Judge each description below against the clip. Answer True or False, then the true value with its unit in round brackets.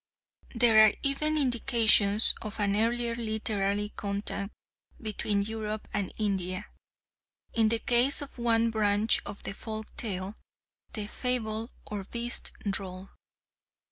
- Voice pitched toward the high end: True (215 Hz)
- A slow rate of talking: True (120 wpm)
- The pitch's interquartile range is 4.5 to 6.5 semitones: False (2.4 semitones)